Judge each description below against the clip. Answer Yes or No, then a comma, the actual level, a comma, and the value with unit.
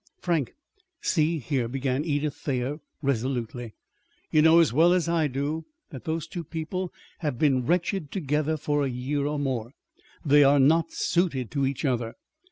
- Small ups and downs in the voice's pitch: No, average, 3.4 semitones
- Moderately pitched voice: Yes, medium, 145 Hz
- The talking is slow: No, average, 165 wpm